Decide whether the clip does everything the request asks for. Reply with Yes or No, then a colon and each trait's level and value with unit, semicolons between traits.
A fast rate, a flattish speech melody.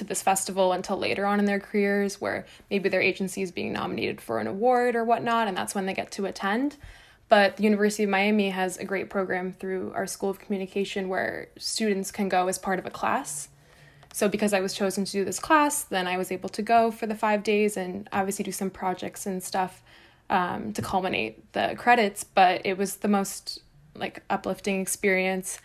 Yes: fast, 210 wpm; narrow, 1.8 semitones